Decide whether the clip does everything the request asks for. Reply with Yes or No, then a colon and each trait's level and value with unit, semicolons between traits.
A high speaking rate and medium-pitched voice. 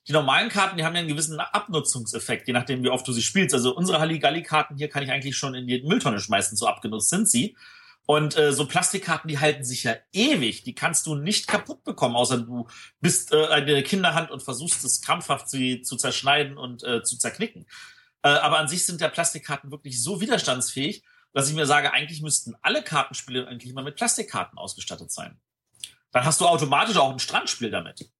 Yes: fast, 205 wpm; medium, 150 Hz